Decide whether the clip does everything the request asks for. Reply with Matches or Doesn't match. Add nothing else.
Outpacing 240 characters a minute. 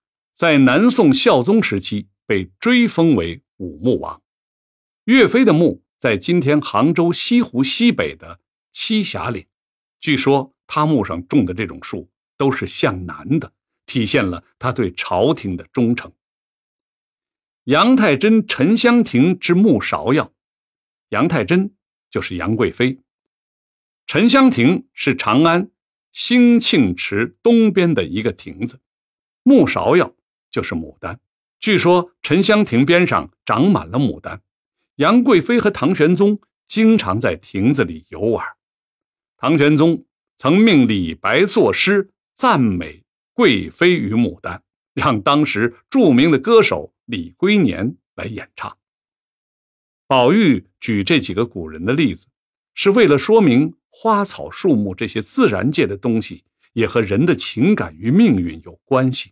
Doesn't match